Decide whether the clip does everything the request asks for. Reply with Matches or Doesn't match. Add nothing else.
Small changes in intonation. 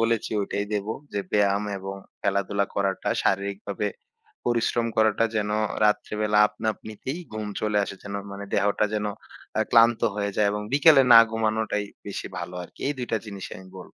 Matches